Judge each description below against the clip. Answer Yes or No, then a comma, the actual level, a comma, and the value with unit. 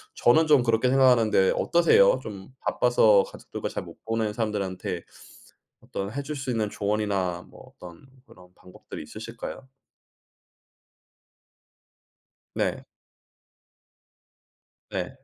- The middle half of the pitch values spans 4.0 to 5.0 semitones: Yes, average, 4.7 semitones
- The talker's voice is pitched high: No, low, 110 Hz